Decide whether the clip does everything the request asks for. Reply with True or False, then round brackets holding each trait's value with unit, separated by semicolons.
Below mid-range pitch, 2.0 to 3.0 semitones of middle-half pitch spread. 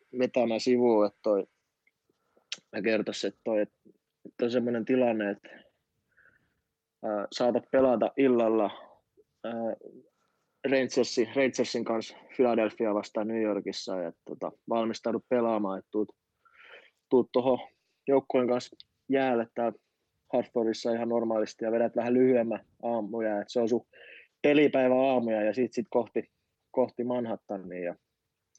True (115 Hz; 2.4 semitones)